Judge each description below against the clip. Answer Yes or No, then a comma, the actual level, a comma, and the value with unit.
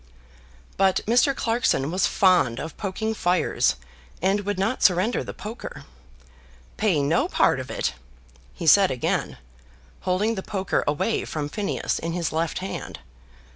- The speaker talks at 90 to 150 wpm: Yes, average, 140 wpm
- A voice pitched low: No, high, 190 Hz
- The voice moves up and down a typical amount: Yes, average, 4.1 semitones